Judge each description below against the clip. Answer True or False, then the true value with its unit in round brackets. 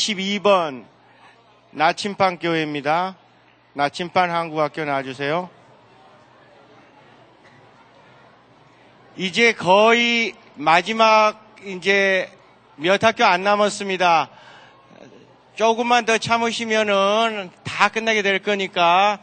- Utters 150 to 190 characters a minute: True (175 characters per minute)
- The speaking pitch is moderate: False (195 Hz)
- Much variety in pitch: False (4.1 semitones)